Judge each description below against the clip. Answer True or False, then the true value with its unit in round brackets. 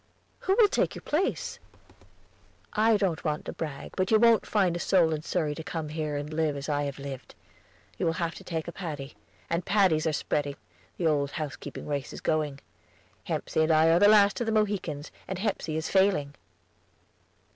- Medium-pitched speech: True (160 Hz)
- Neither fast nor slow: True (195 wpm)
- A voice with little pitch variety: False (4.6 semitones)